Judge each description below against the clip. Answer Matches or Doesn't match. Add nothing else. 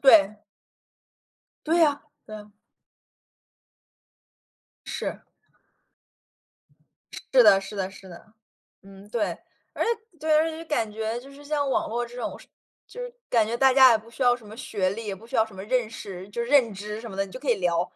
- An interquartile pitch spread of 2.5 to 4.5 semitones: Doesn't match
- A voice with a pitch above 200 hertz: Matches